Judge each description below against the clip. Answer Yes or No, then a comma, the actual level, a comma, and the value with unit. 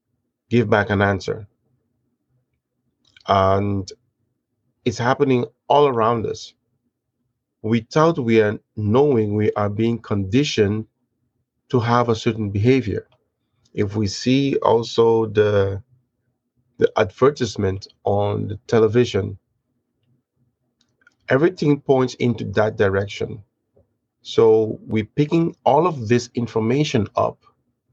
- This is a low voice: Yes, low, 120 Hz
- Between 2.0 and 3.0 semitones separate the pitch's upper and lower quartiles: Yes, narrow, 2.4 semitones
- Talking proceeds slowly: Yes, slow, 100 wpm